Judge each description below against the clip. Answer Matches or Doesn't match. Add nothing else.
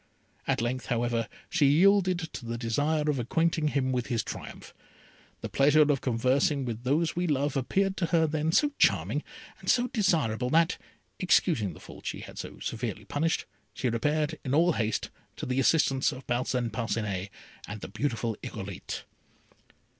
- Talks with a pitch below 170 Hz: Matches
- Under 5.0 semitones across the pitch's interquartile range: Doesn't match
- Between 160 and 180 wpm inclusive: Matches